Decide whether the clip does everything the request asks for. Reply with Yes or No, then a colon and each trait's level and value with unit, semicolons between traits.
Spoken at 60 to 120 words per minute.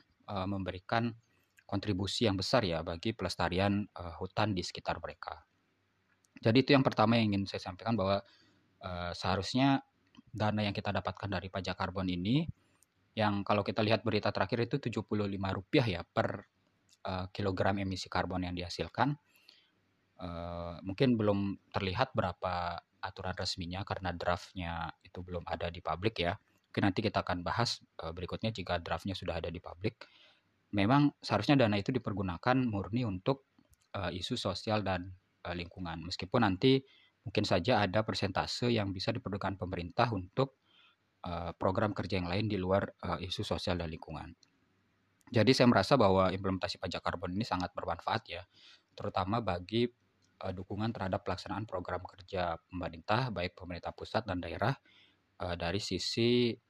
No: average, 135 wpm